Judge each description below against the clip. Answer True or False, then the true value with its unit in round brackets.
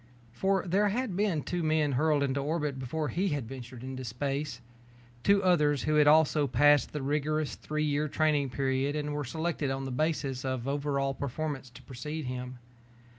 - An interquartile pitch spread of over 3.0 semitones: False (2.7 semitones)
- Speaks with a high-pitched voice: False (145 Hz)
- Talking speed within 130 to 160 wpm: False (175 wpm)